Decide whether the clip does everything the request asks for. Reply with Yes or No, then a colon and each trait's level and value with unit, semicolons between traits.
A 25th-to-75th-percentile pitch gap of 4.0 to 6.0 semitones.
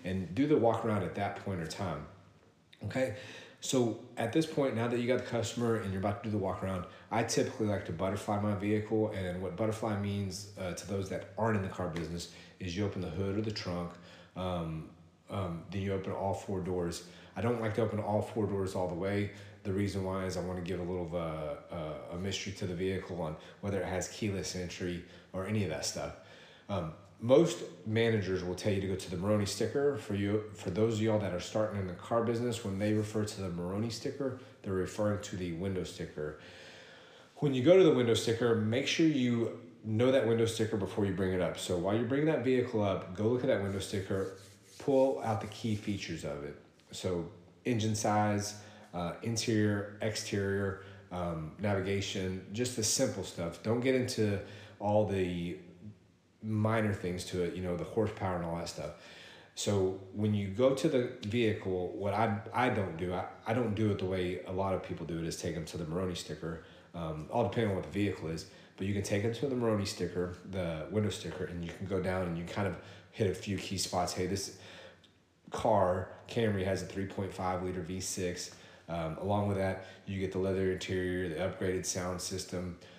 No: average, 3.1 semitones